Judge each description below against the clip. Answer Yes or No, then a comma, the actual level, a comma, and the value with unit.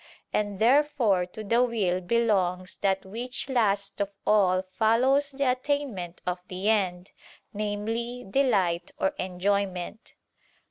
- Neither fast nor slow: No, slow, 120 wpm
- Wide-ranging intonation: No, average, 4.3 semitones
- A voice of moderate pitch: No, high, 205 Hz